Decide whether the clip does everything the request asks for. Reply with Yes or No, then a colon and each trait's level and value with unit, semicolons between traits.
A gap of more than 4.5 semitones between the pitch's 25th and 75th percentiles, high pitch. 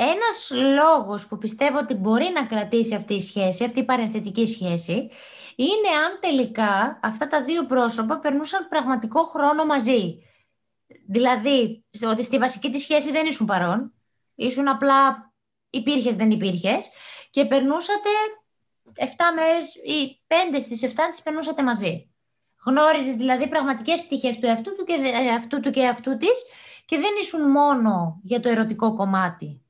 Yes: wide, 5.5 semitones; very high, 260 Hz